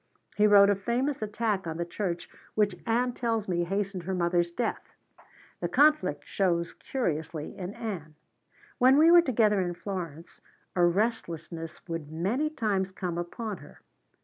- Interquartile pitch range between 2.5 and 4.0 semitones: No, average, 4.7 semitones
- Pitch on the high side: Yes, high, 195 Hz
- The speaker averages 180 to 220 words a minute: No, average, 150 wpm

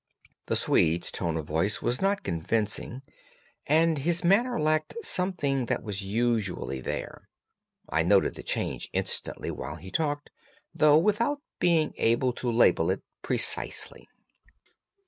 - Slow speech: Yes, slow, 130 wpm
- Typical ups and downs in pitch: No, wide, 8.9 semitones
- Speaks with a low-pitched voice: Yes, low, 125 Hz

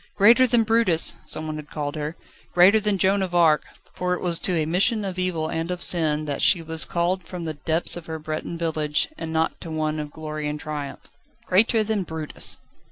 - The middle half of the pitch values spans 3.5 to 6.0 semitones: No, average, 3.1 semitones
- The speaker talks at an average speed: No, fast, 210 wpm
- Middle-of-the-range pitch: Yes, medium, 165 Hz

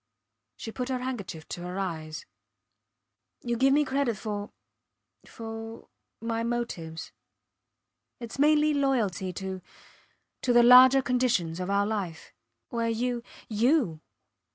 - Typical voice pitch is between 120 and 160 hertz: No, high, 230 Hz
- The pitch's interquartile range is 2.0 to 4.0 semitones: No, average, 4.8 semitones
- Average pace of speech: No, slow, 120 wpm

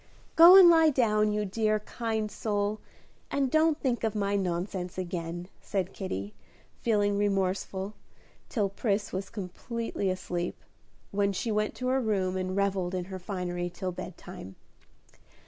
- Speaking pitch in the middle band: No, high, 200 Hz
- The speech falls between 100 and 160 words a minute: Yes, average, 145 wpm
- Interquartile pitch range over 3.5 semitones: No, average, 3.0 semitones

